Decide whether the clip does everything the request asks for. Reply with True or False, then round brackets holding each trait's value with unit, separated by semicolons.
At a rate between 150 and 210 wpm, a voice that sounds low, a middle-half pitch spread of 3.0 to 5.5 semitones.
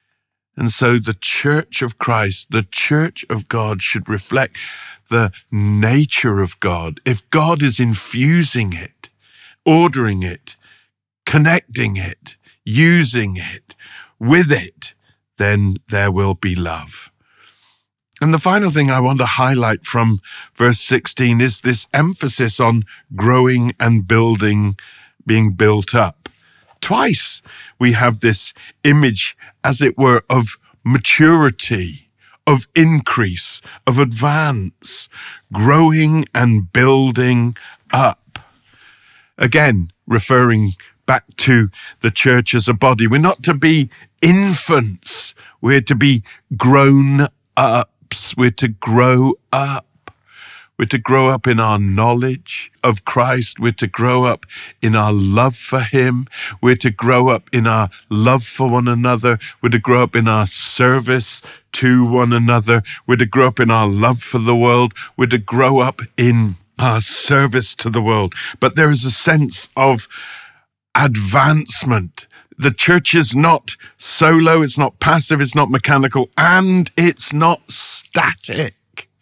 False (135 wpm; 125 Hz; 3.7 semitones)